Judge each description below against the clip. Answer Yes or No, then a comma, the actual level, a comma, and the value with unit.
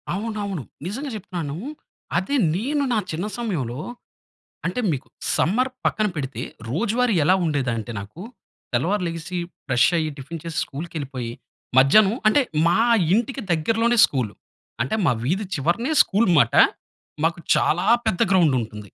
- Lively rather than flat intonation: Yes, wide, 7.7 semitones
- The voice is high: No, medium, 175 Hz